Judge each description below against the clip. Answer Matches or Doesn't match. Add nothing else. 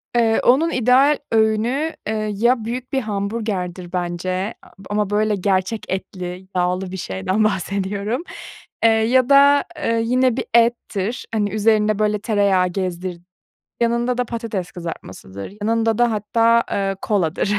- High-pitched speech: Matches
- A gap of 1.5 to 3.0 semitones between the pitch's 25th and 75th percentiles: Doesn't match